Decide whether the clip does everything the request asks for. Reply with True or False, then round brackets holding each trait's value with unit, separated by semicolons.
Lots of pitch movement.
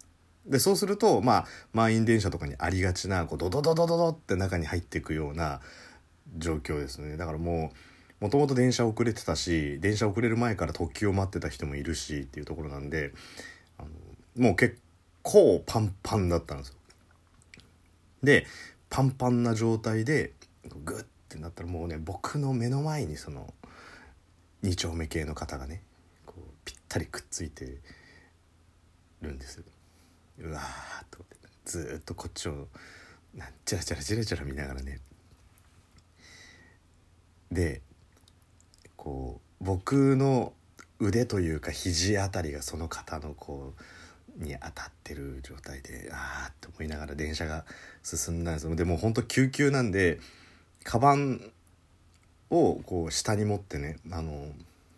False (3.7 semitones)